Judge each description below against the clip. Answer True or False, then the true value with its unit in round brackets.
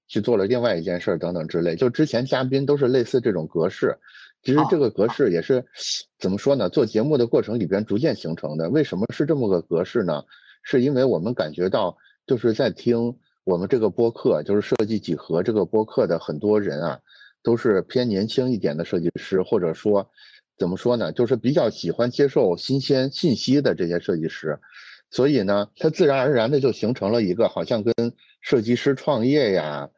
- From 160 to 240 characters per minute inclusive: False (310 characters per minute)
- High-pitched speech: False (115 Hz)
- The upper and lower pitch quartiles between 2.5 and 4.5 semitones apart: False (5.5 semitones)